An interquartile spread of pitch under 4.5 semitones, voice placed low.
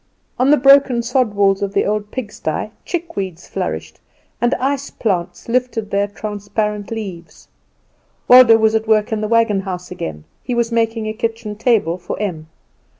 No: average, 3.1 semitones; high, 215 Hz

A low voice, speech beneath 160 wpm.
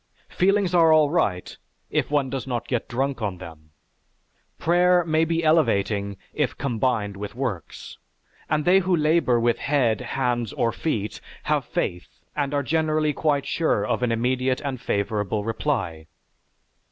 Yes: low, 130 Hz; average, 150 wpm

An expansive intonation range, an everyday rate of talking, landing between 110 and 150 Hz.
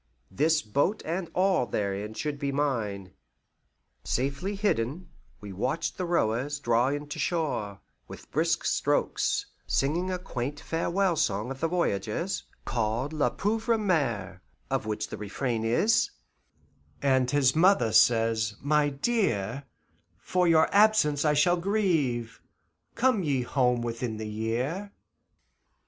No: wide, 7.2 semitones; slow, 130 wpm; medium, 140 Hz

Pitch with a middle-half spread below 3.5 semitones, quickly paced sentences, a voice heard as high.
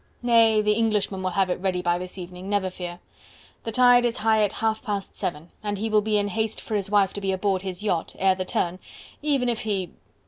Yes: average, 2.9 semitones; fast, 235 wpm; high, 205 Hz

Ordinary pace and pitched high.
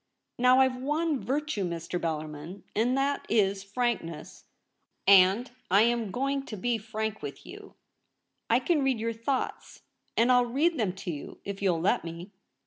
Yes: average, 165 wpm; high, 225 Hz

